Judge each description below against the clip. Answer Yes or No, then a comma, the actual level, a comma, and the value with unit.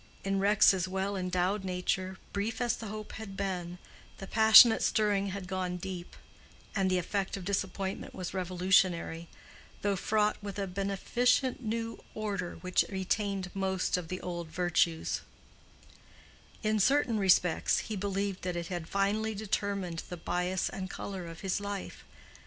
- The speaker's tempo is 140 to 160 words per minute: Yes, average, 145 wpm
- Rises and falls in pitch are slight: Yes, narrow, 2.0 semitones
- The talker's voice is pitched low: No, high, 195 Hz